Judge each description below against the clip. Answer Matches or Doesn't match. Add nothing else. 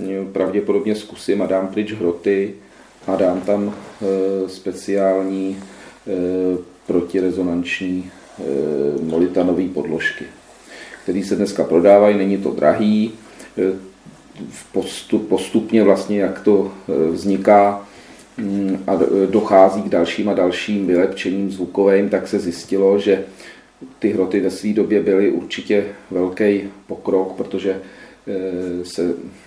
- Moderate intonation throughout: Doesn't match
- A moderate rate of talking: Doesn't match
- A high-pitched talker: Doesn't match